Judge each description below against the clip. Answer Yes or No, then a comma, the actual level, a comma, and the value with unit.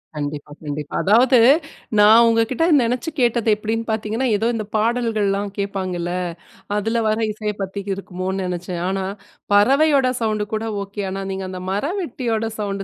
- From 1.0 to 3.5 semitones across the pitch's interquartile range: Yes, average, 3.1 semitones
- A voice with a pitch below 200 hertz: No, high, 210 Hz